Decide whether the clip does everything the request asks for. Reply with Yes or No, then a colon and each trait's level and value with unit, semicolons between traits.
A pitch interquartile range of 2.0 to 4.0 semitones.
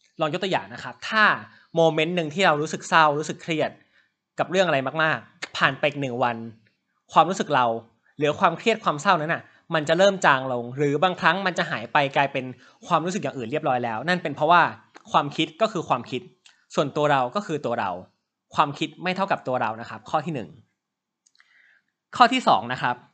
No: average, 5.0 semitones